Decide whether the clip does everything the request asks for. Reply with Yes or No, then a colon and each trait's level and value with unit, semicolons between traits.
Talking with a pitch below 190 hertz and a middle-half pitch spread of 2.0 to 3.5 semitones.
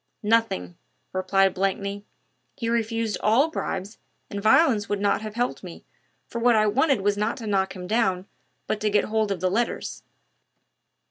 No: high, 210 Hz; narrow, 2.6 semitones